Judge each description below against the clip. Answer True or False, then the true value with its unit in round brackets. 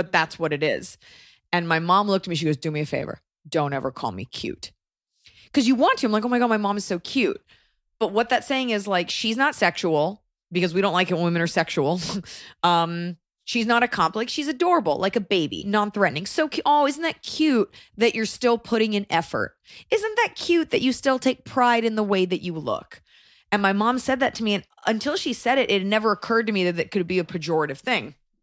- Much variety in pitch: True (6.0 semitones)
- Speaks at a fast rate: True (245 wpm)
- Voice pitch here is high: True (210 Hz)